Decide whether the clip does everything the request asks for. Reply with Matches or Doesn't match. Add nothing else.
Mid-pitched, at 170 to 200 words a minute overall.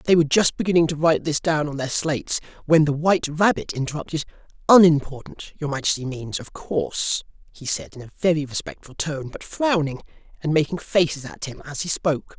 Matches